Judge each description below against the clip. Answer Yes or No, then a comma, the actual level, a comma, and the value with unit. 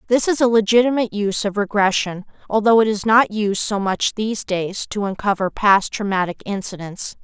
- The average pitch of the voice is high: Yes, high, 205 Hz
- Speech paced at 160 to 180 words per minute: Yes, average, 175 wpm